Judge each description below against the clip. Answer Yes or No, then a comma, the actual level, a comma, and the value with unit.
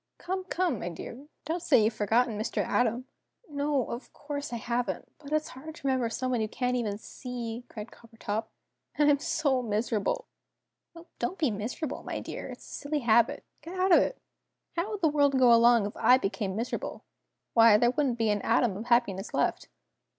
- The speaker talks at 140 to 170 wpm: No, average, 195 wpm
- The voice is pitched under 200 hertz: No, high, 245 Hz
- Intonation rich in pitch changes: No, average, 4.5 semitones